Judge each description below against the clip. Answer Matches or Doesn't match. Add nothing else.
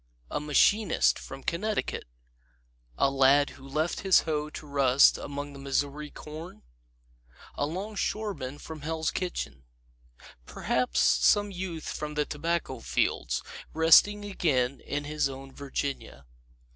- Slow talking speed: Matches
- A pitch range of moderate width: Matches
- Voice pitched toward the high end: Doesn't match